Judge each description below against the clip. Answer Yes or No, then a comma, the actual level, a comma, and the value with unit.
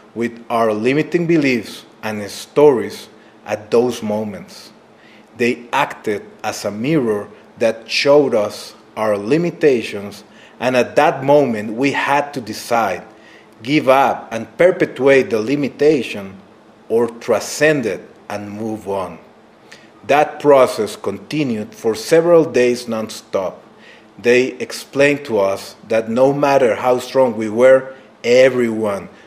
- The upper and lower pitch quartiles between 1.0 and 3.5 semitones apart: No, average, 4.5 semitones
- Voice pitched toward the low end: Yes, low, 120 Hz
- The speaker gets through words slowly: Yes, slow, 120 wpm